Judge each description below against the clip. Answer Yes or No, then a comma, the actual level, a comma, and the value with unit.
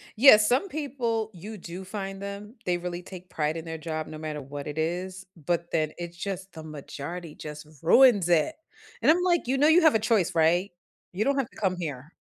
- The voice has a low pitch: No, medium, 180 Hz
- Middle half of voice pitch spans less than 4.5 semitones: No, average, 5.2 semitones